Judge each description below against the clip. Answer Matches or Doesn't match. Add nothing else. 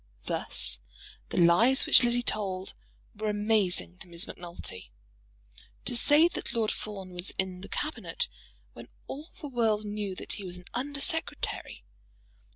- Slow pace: Doesn't match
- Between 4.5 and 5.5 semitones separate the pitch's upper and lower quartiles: Matches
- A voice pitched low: Doesn't match